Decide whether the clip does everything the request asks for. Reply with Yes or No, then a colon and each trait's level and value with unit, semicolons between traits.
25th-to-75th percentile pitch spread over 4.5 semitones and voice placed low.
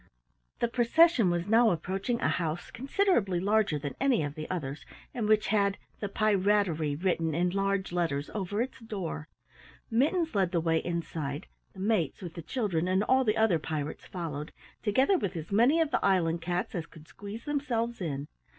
No: wide, 5.4 semitones; high, 195 Hz